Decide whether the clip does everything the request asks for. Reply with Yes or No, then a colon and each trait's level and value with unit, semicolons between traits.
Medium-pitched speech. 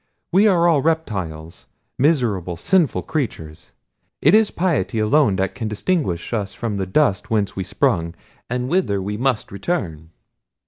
No: low, 110 Hz